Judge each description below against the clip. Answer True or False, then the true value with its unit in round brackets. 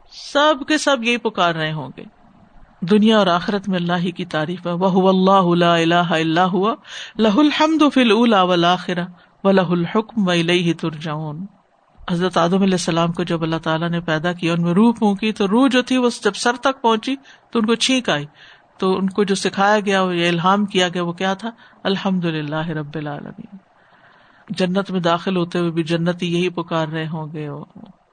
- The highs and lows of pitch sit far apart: False (4.0 semitones)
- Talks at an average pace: True (165 wpm)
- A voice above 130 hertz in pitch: True (185 Hz)